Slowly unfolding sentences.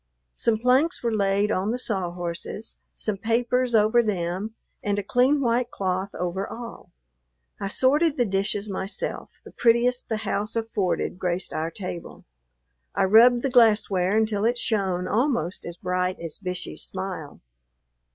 No: average, 150 wpm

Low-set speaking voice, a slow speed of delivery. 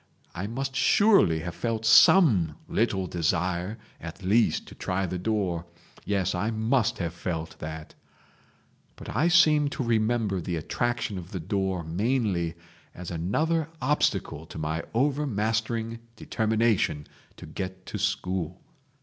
Yes: low, 100 Hz; slow, 130 wpm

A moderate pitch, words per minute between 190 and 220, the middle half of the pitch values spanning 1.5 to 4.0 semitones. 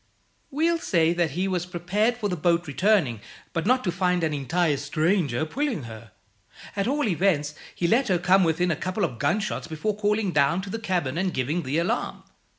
No: medium, 180 Hz; average, 195 wpm; average, 4.5 semitones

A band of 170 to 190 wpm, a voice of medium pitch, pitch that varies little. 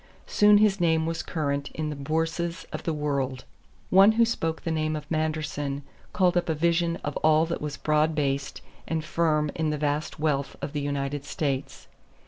Yes: average, 185 wpm; medium, 155 Hz; narrow, 2.2 semitones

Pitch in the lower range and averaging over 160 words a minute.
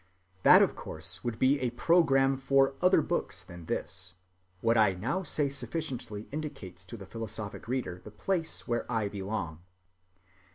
No: low, 120 Hz; average, 155 wpm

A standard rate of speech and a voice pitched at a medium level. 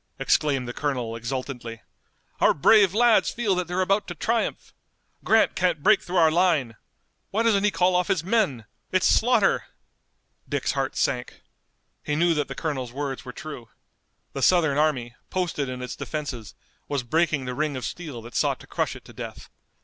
Yes: average, 180 wpm; medium, 150 Hz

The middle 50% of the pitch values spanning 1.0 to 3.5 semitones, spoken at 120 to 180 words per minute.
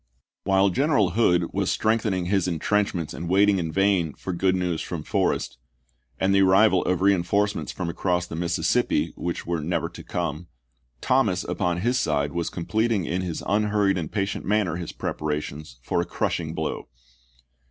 Yes: average, 2.8 semitones; average, 165 wpm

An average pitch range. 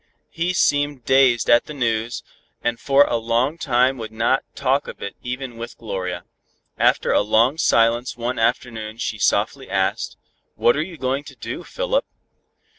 Yes: average, 3.3 semitones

